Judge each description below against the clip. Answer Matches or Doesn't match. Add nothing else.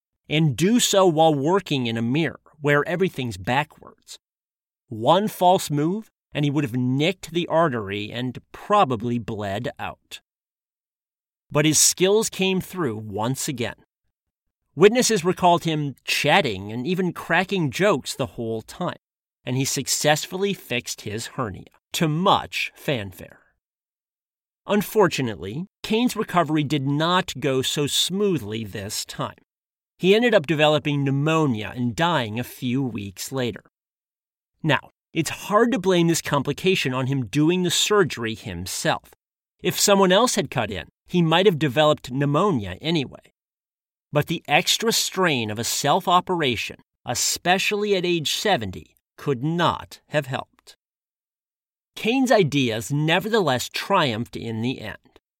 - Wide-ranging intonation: Matches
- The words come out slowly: Matches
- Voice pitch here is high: Doesn't match